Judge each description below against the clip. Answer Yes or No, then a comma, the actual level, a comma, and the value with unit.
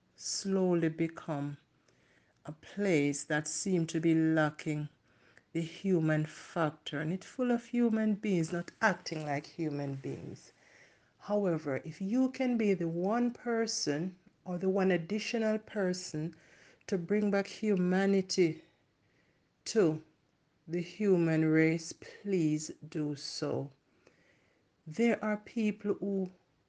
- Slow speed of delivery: Yes, slow, 115 wpm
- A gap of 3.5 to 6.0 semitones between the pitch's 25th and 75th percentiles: Yes, average, 4.6 semitones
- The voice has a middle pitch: Yes, medium, 175 Hz